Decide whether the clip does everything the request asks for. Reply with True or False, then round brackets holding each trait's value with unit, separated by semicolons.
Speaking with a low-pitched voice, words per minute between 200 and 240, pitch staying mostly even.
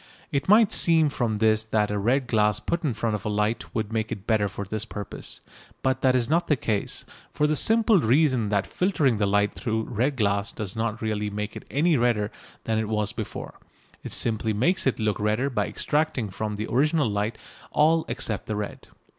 False (110 Hz; 205 wpm; 4.8 semitones)